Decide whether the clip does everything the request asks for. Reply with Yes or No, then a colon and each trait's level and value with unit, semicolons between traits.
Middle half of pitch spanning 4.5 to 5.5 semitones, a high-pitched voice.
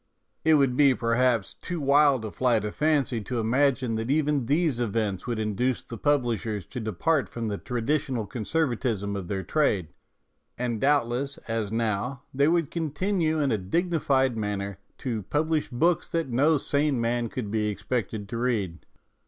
No: average, 4.8 semitones; low, 125 Hz